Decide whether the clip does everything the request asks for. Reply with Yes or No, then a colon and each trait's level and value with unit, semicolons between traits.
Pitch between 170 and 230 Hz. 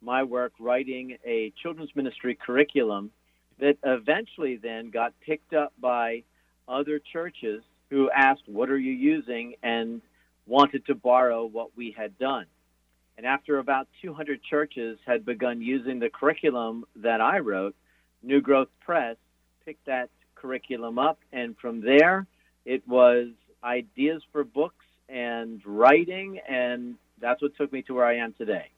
No: low, 125 Hz